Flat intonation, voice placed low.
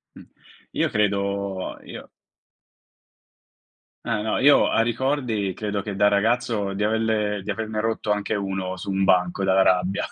Yes: narrow, 2.3 semitones; low, 105 Hz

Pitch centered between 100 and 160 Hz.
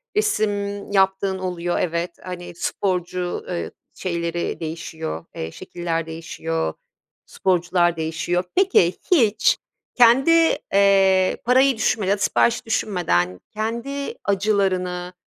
No: medium, 185 Hz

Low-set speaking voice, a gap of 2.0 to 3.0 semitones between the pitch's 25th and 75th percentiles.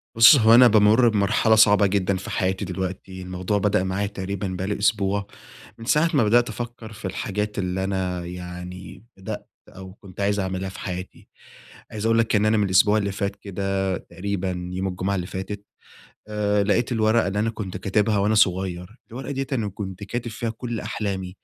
Yes: low, 100 Hz; narrow, 2.5 semitones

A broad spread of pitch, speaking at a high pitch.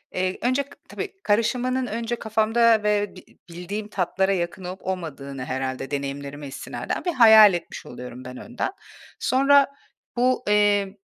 Yes: wide, 6.1 semitones; high, 205 Hz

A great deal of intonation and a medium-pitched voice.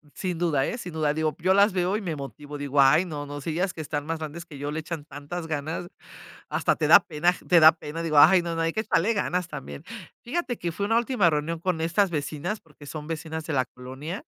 No: average, 3.2 semitones; medium, 160 Hz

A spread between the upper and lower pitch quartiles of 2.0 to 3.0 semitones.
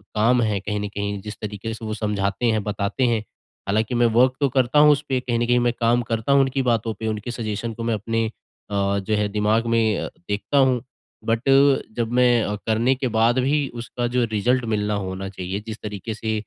Yes: narrow, 2.6 semitones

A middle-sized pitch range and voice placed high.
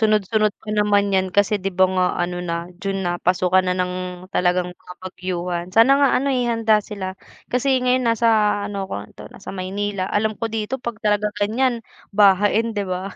Yes: average, 3.0 semitones; high, 205 Hz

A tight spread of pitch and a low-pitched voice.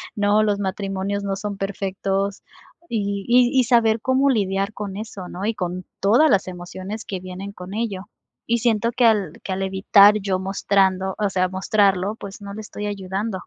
No: narrow, 2.0 semitones; high, 200 Hz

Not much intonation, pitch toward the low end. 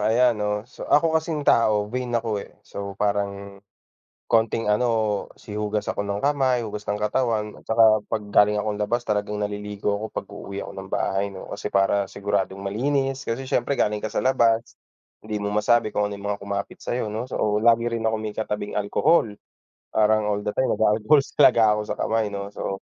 Yes: narrow, 2.2 semitones; low, 105 Hz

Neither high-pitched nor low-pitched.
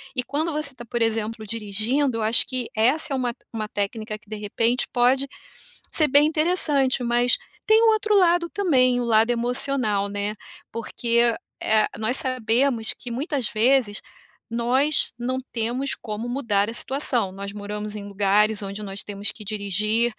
No: high, 235 Hz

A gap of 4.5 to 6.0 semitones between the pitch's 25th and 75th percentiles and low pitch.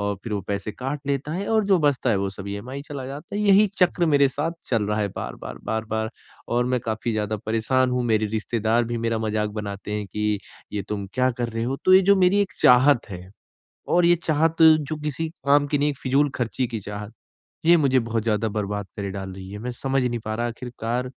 Yes: average, 5.3 semitones; low, 120 Hz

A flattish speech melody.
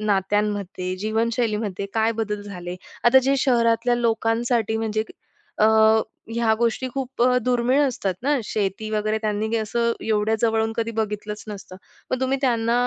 Yes: narrow, 2.1 semitones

